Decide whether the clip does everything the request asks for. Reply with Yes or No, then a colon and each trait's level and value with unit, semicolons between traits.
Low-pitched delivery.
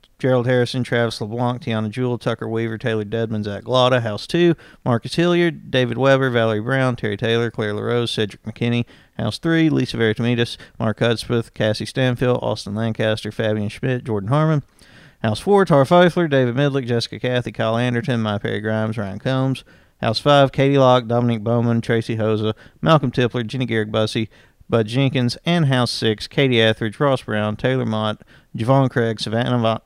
Yes: low, 120 Hz